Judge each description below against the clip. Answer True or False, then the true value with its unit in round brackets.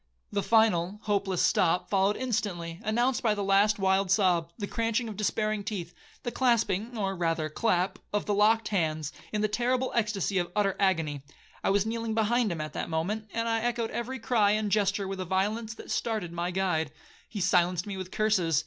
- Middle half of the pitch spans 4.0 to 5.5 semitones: False (3.5 semitones)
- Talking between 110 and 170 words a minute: False (190 wpm)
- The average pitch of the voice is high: True (205 Hz)